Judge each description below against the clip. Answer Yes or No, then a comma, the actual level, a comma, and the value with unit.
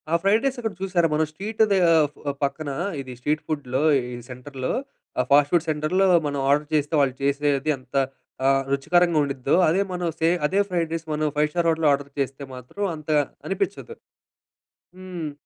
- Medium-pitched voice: Yes, medium, 155 Hz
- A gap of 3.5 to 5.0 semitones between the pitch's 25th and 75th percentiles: Yes, average, 3.9 semitones